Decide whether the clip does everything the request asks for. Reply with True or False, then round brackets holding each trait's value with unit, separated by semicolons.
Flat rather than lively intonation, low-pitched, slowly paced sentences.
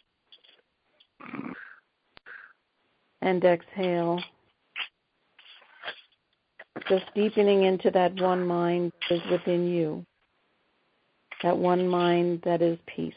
False (1.4 semitones; 175 Hz; 80 wpm)